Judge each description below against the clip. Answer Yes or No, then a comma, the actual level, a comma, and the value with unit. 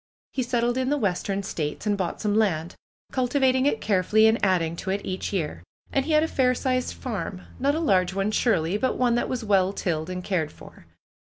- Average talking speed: No, fast, 215 wpm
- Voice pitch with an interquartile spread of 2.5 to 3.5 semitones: No, wide, 5.5 semitones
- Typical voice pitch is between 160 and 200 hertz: No, high, 210 Hz